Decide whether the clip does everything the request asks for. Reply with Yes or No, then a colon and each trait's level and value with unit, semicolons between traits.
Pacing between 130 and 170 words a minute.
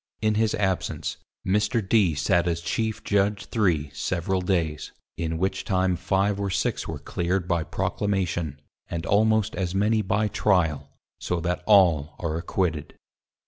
Yes: average, 150 wpm